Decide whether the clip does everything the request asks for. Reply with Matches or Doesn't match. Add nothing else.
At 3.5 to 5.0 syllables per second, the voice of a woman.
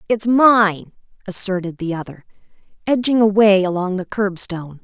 Matches